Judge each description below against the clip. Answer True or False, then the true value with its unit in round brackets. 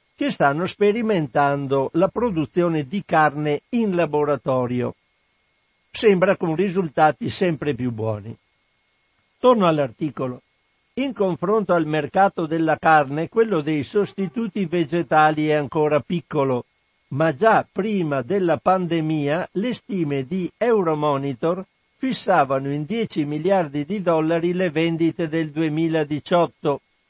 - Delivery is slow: True (110 wpm)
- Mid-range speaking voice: True (165 Hz)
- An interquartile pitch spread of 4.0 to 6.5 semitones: True (4.5 semitones)